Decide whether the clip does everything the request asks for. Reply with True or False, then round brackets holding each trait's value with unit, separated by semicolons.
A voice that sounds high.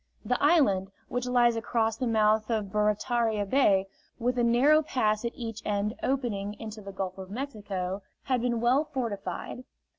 True (225 Hz)